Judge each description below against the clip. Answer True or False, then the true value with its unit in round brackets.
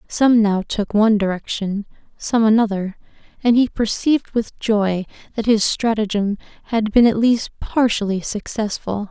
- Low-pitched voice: False (215 Hz)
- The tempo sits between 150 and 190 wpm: False (140 wpm)